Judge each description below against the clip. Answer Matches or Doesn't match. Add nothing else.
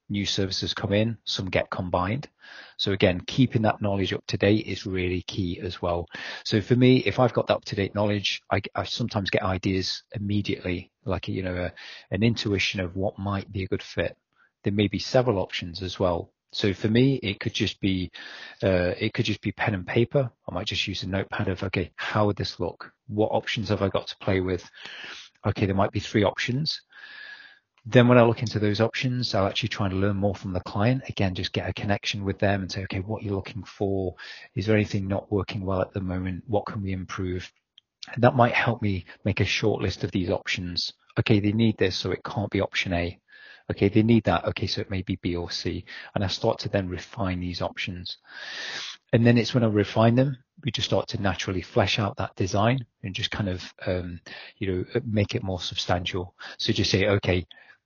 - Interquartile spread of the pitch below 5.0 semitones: Matches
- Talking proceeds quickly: Matches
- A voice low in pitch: Matches